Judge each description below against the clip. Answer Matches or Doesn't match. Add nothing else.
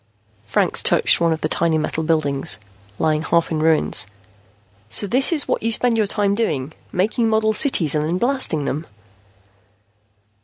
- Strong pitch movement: Matches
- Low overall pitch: Doesn't match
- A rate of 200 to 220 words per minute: Doesn't match